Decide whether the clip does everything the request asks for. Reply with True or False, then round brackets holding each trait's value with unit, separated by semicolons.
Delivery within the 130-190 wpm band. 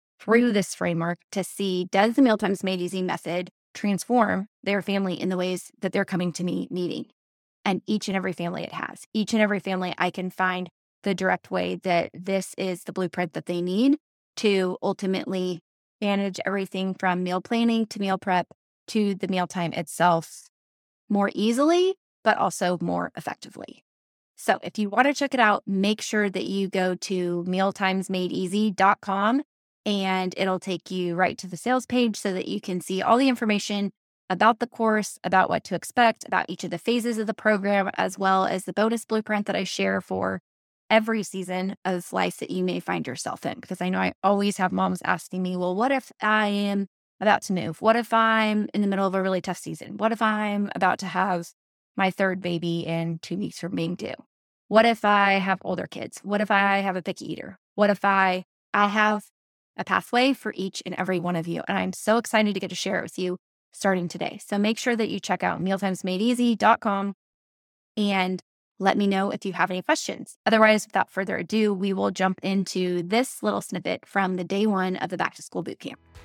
False (200 wpm)